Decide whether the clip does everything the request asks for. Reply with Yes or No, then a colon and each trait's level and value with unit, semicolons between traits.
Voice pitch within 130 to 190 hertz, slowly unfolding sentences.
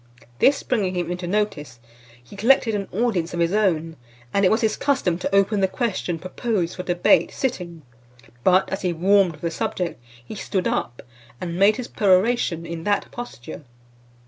No: medium, 185 Hz; average, 175 wpm